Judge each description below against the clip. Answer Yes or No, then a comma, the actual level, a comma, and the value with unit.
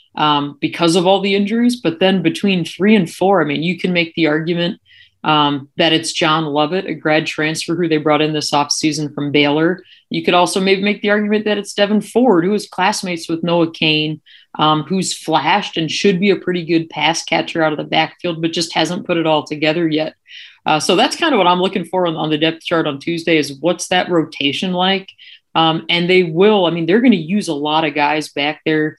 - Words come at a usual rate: No, fast, 230 wpm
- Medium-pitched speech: Yes, medium, 170 Hz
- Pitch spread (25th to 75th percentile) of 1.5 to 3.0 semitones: No, average, 3.5 semitones